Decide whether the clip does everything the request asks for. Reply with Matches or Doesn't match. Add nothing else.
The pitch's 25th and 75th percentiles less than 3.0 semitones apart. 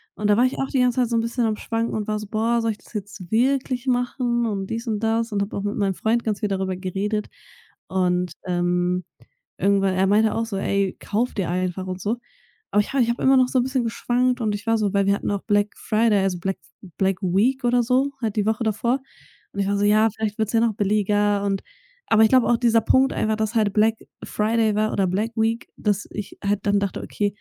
Matches